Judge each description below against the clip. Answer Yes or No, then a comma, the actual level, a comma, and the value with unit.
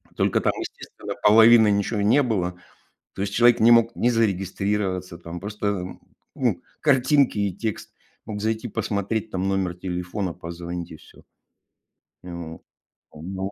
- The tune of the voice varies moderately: Yes, average, 3.7 semitones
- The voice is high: No, low, 100 Hz